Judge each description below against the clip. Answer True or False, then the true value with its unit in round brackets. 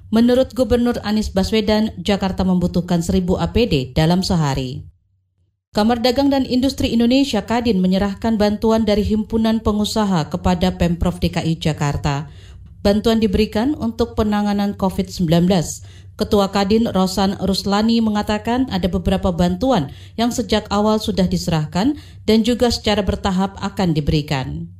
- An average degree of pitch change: True (4.2 semitones)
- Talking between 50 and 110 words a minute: False (120 wpm)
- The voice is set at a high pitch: True (200 Hz)